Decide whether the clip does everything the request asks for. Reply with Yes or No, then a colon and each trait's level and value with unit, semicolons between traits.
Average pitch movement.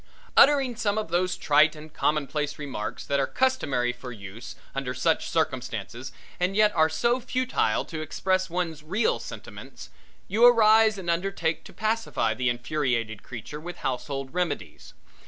No: wide, 7.3 semitones